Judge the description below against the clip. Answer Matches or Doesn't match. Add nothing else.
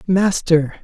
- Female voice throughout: Doesn't match